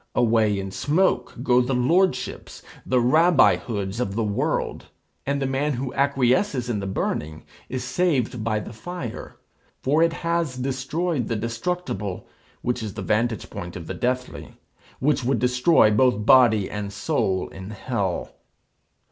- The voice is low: Yes, low, 125 Hz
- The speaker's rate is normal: Yes, average, 150 wpm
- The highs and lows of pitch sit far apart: No, average, 4.3 semitones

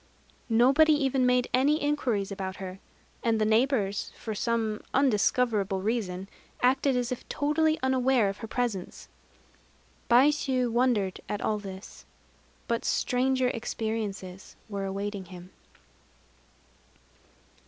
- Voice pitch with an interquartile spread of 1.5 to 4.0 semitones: No, average, 4.5 semitones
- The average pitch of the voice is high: Yes, high, 230 Hz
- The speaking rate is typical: No, slow, 110 wpm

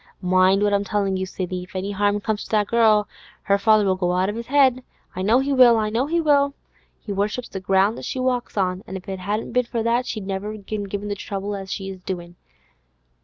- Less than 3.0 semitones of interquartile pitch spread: No, average, 3.3 semitones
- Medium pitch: No, high, 205 Hz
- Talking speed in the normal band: No, fast, 245 wpm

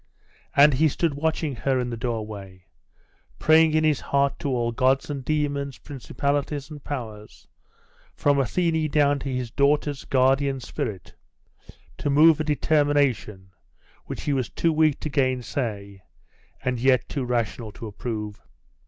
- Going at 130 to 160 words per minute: Yes, average, 145 wpm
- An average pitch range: Yes, average, 3.6 semitones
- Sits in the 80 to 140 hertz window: Yes, low, 135 Hz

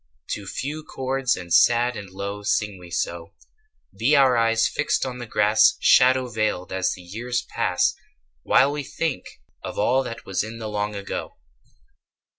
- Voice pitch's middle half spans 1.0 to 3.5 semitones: No, average, 4.2 semitones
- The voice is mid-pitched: No, low, 115 Hz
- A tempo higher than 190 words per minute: No, average, 165 wpm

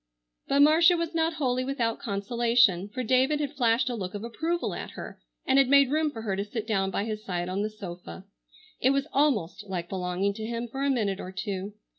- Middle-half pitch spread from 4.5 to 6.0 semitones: Yes, wide, 5.6 semitones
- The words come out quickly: Yes, fast, 220 wpm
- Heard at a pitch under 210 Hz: No, high, 230 Hz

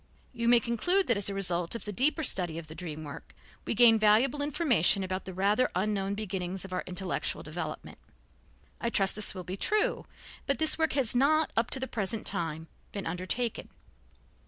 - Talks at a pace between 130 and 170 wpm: No, average, 190 wpm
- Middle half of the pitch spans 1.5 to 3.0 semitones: No, average, 5.0 semitones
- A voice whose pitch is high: Yes, high, 205 Hz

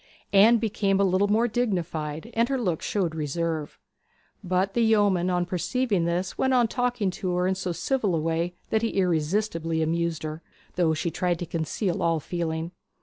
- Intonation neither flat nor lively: Yes, average, 4.1 semitones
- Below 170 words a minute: No, average, 180 wpm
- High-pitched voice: No, medium, 180 Hz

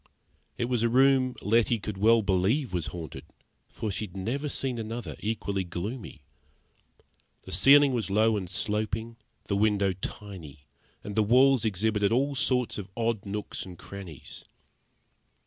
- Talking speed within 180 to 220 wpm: No, average, 145 wpm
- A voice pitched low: Yes, low, 110 Hz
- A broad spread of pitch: No, average, 3.5 semitones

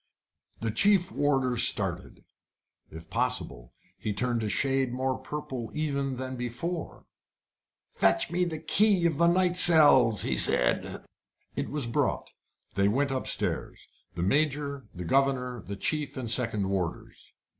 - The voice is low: Yes, low, 130 Hz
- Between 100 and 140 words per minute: Yes, slow, 135 wpm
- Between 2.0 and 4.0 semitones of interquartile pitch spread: No, average, 5.1 semitones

